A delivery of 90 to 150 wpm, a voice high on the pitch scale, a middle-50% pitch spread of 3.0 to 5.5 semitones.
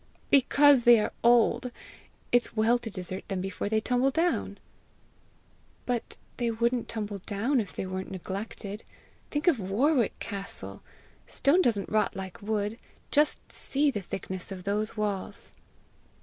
Yes: average, 140 wpm; high, 220 Hz; average, 3.9 semitones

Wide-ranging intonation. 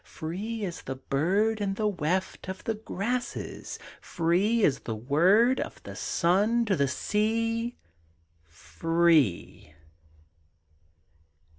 Yes: wide, 6.2 semitones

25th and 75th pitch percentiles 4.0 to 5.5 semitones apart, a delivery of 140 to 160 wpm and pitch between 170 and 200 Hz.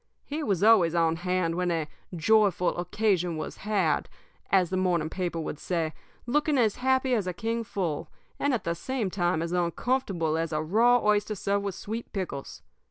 No: average, 4.7 semitones; average, 180 wpm; medium, 185 Hz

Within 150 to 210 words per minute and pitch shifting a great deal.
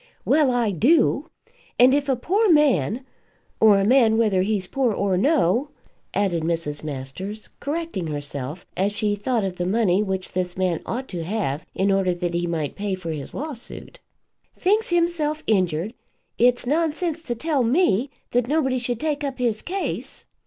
Yes: average, 165 wpm; wide, 7.3 semitones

